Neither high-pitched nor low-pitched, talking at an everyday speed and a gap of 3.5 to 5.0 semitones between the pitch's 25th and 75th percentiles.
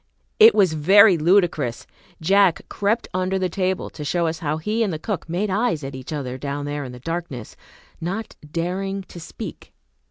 Yes: medium, 175 Hz; average, 185 wpm; average, 4.5 semitones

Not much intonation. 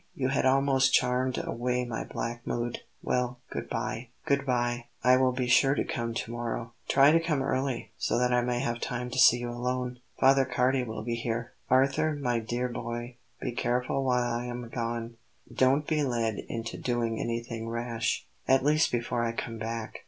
Yes: narrow, 1.8 semitones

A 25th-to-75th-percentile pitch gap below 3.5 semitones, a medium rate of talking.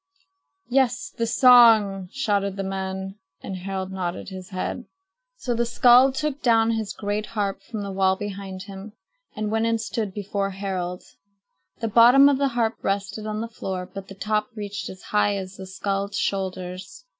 Yes: average, 2.9 semitones; average, 170 wpm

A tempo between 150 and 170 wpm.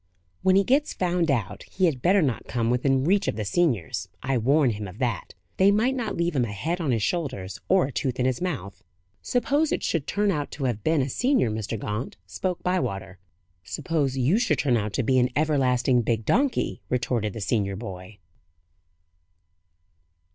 No: average, 190 wpm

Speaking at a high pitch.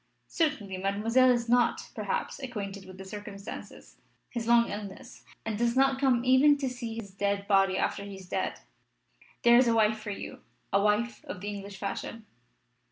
Yes: high, 215 Hz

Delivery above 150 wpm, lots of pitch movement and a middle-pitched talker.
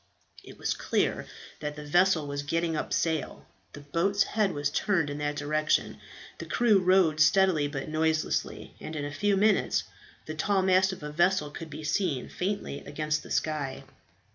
No: average, 175 wpm; average, 4.2 semitones; medium, 155 Hz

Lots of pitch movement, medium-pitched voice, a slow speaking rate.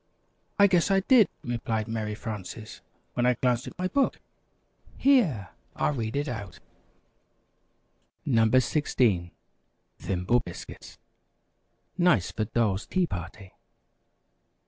No: wide, 6.7 semitones; low, 120 Hz; slow, 125 wpm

